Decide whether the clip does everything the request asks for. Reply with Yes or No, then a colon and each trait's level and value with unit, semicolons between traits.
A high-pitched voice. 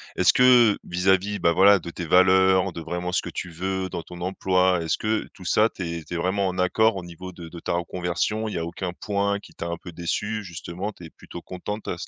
No: very low, 90 Hz